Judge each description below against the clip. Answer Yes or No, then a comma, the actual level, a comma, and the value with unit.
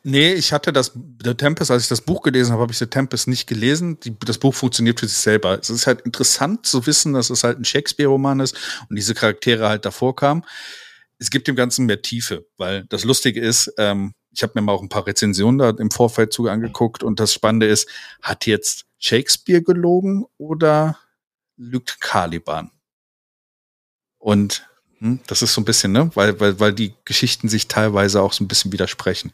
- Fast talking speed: Yes, fast, 200 wpm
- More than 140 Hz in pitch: No, low, 120 Hz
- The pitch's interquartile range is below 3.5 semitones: No, average, 4.1 semitones